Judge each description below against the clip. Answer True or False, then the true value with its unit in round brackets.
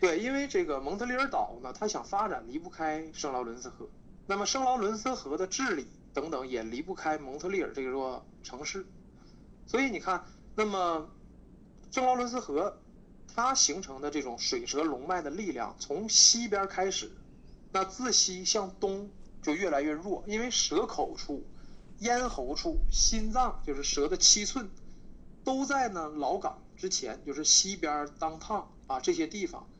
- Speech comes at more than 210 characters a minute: True (245 characters per minute)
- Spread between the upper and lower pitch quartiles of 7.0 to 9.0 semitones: True (7.8 semitones)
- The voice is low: False (195 Hz)